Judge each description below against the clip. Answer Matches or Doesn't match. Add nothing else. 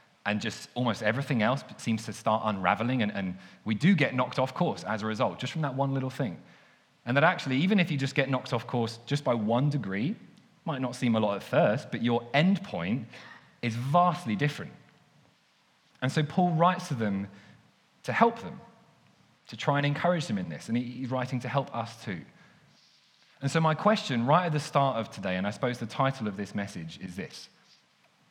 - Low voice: Matches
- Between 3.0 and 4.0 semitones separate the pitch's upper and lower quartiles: Doesn't match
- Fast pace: Matches